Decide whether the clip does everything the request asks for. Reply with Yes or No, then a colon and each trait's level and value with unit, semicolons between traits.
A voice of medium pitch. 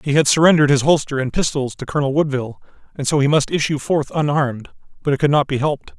Yes: medium, 145 Hz